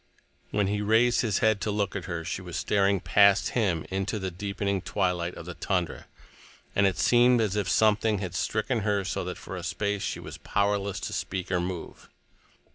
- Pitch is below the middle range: Yes, low, 100 Hz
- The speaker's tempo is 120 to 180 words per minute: No, average, 200 wpm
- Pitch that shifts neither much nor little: No, narrow, 2.3 semitones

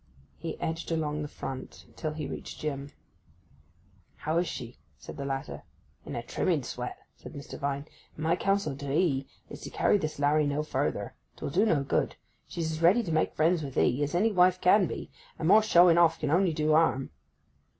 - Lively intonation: No, average, 3.4 semitones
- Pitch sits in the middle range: Yes, medium, 155 Hz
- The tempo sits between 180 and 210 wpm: Yes, average, 200 wpm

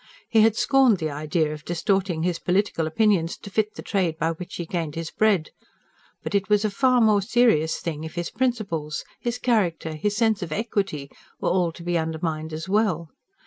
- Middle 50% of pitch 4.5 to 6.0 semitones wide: Yes, average, 4.9 semitones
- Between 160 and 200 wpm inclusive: Yes, average, 195 wpm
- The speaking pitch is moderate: Yes, medium, 180 Hz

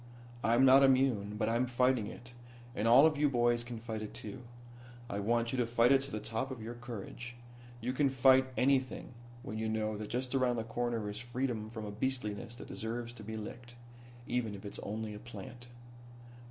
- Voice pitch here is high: No, low, 120 Hz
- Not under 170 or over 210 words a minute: Yes, fast, 205 wpm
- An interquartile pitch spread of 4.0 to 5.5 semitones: No, average, 2.7 semitones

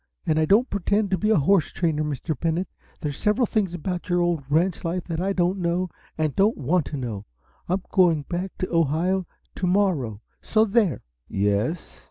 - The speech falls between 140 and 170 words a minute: No, average, 190 wpm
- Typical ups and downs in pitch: Yes, average, 3.7 semitones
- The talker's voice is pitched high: No, medium, 175 Hz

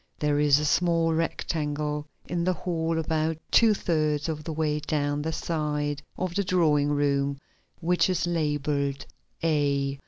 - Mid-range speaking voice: Yes, medium, 150 Hz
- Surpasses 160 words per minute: No, average, 150 wpm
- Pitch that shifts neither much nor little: No, narrow, 2.2 semitones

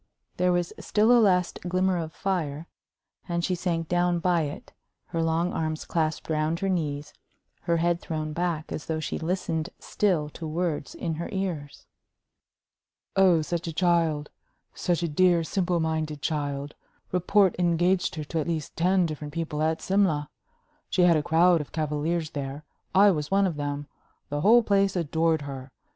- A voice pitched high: No, medium, 165 Hz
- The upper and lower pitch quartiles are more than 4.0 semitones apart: No, average, 2.7 semitones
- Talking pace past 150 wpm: Yes, average, 170 wpm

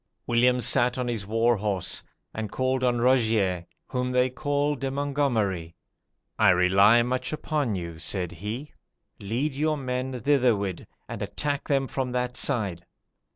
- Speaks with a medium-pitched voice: No, low, 125 Hz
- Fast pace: No, average, 145 wpm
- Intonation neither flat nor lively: Yes, average, 4.6 semitones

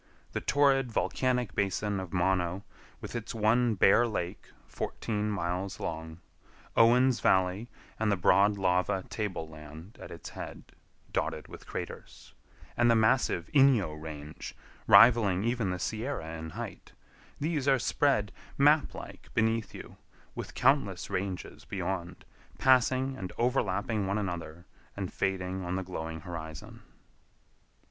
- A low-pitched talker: Yes, low, 100 Hz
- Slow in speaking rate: Yes, slow, 130 wpm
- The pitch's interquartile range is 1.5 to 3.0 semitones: No, average, 4.8 semitones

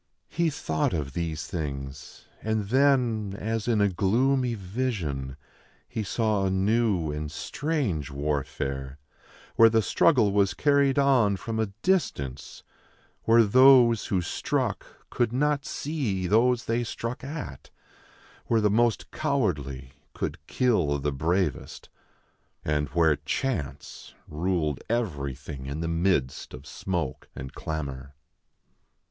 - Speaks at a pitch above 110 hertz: No, very low, 95 Hz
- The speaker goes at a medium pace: No, slow, 120 wpm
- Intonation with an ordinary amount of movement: No, wide, 8.1 semitones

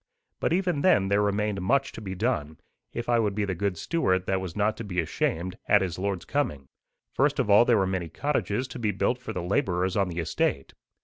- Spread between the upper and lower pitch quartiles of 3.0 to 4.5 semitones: Yes, average, 4.0 semitones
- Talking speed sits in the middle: No, fast, 230 wpm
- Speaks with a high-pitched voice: No, low, 100 Hz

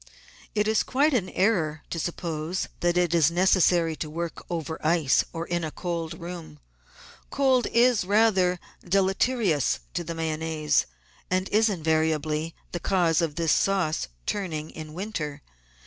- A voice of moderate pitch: Yes, medium, 170 Hz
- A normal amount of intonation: Yes, average, 3.3 semitones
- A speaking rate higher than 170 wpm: No, average, 150 wpm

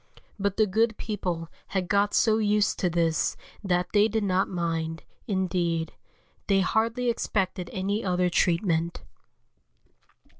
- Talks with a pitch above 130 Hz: Yes, high, 190 Hz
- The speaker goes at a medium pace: No, slow, 125 wpm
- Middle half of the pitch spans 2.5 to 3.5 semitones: Yes, average, 3.2 semitones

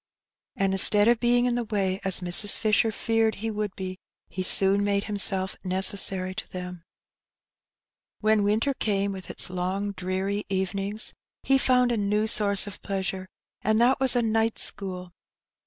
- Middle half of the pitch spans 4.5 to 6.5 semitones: No, narrow, 2.5 semitones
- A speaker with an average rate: Yes, average, 170 wpm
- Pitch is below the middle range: No, high, 200 Hz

